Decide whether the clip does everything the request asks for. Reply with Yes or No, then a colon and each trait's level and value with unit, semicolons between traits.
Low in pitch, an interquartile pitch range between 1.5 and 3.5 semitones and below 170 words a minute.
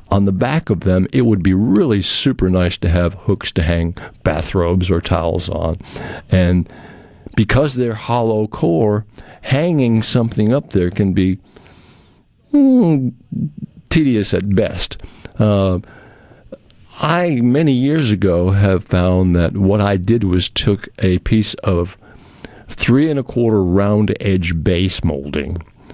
No: low, 100 Hz; average, 4.3 semitones; slow, 135 wpm